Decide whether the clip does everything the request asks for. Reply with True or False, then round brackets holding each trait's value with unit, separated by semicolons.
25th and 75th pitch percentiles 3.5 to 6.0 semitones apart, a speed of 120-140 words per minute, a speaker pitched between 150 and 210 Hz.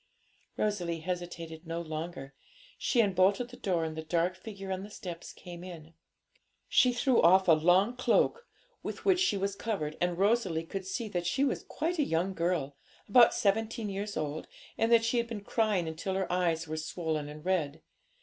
False (4.4 semitones; 185 wpm; 185 Hz)